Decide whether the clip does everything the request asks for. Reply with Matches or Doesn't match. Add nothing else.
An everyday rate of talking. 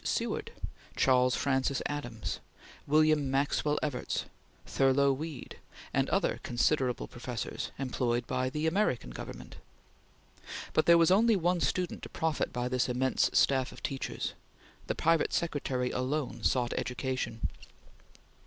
Doesn't match